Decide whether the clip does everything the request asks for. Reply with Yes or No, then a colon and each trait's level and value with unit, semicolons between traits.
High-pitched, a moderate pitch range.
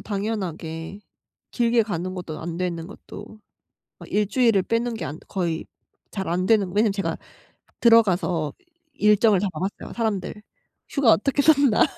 Yes: high, 205 Hz; average, 4.1 semitones